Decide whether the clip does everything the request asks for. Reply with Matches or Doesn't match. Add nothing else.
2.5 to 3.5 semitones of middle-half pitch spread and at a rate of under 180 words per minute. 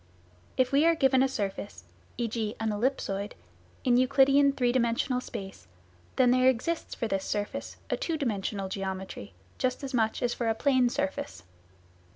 Doesn't match